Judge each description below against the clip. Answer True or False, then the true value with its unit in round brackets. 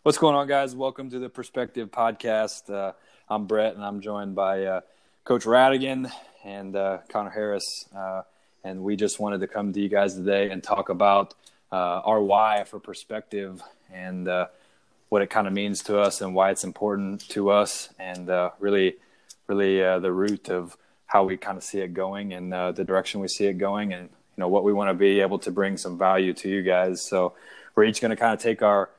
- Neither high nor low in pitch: False (100 Hz)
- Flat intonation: True (2.0 semitones)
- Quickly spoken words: True (215 wpm)